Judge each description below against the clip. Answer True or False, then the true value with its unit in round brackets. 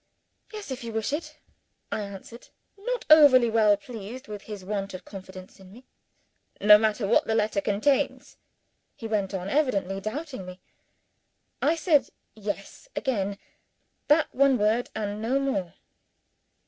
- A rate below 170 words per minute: True (145 wpm)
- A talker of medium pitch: False (215 Hz)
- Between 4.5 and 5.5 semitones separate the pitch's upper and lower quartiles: True (5.0 semitones)